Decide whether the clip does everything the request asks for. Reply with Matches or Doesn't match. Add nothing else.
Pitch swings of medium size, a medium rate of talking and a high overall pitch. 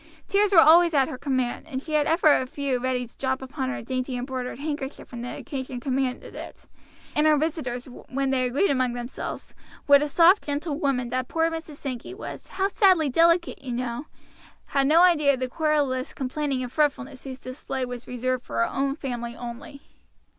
Matches